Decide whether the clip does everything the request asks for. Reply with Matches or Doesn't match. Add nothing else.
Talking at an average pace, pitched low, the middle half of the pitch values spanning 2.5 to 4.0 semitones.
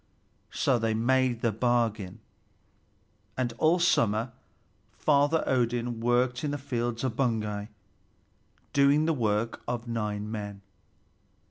Doesn't match